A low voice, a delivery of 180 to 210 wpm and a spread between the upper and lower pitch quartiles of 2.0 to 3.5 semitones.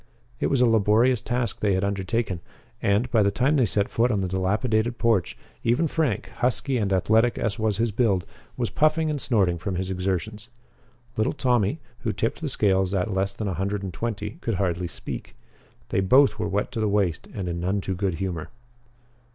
No: low, 105 Hz; average, 200 wpm; average, 3.9 semitones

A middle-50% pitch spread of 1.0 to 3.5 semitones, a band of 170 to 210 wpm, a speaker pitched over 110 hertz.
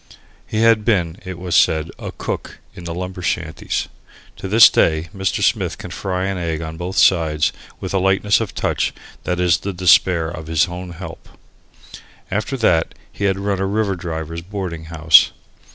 No: average, 2.7 semitones; average, 180 wpm; very low, 90 Hz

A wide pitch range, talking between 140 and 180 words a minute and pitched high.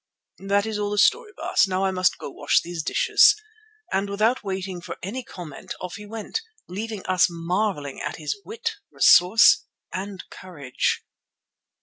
No: average, 3.3 semitones; average, 160 wpm; high, 195 Hz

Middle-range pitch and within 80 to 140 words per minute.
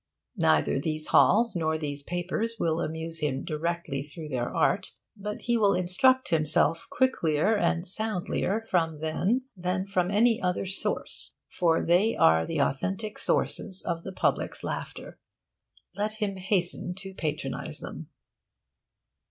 Yes: medium, 180 Hz; slow, 135 wpm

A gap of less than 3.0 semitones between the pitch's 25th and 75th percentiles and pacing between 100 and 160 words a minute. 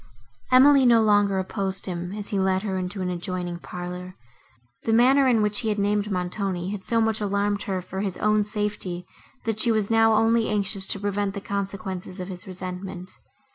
No: narrow, 2.5 semitones; average, 195 wpm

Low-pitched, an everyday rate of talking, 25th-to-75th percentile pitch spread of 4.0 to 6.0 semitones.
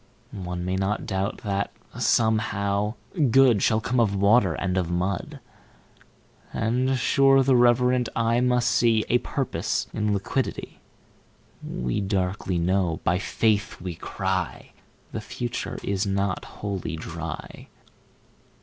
No: low, 105 Hz; slow, 105 wpm; average, 4.3 semitones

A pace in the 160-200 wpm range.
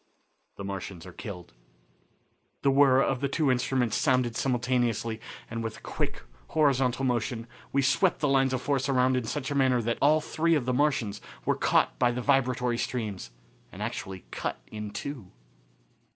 Yes: average, 170 wpm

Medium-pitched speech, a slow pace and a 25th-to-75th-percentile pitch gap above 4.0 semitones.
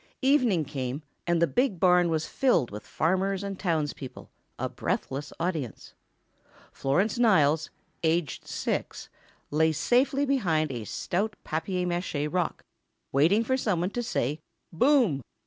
Yes: medium, 170 Hz; slow, 130 wpm; average, 5.2 semitones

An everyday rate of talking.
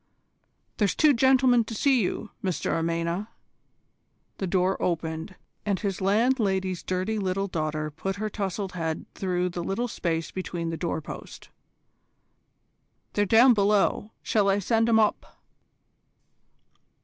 No: slow, 125 wpm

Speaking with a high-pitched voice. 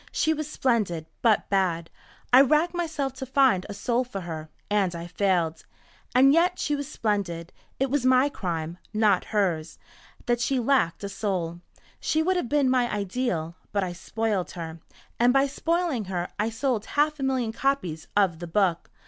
Yes: high, 220 Hz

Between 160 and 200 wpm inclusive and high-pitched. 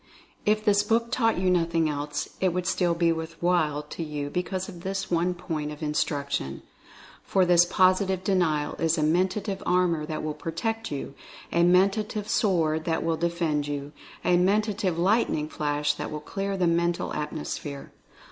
No: average, 175 wpm; medium, 170 Hz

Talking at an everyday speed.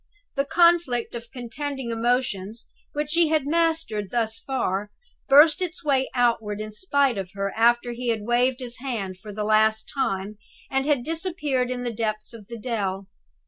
Yes: average, 170 wpm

